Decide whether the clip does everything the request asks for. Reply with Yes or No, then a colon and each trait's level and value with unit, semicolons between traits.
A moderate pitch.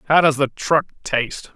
Yes: medium, 145 Hz